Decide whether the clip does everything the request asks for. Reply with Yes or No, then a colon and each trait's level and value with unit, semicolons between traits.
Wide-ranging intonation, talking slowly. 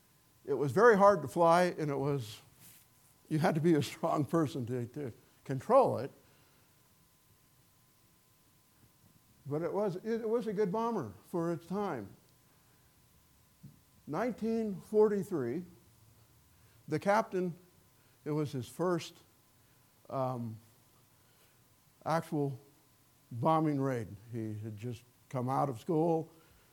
Yes: wide, 5.8 semitones; slow, 110 wpm